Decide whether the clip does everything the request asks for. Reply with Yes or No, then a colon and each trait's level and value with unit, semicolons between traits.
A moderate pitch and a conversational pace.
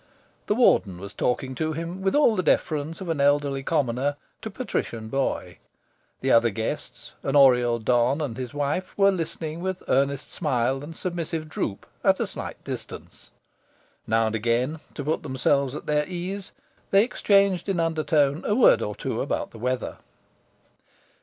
Yes: medium, 145 Hz; average, 160 wpm